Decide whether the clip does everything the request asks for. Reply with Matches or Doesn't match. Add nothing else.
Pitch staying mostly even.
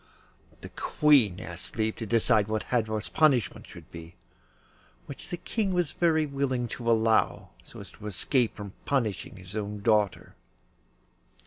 Doesn't match